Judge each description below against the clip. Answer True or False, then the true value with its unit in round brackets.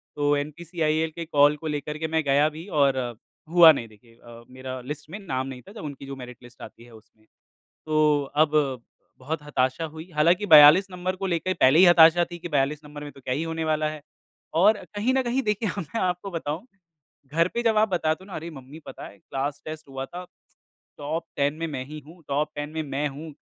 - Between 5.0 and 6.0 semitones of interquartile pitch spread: False (3.6 semitones)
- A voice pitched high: False (155 Hz)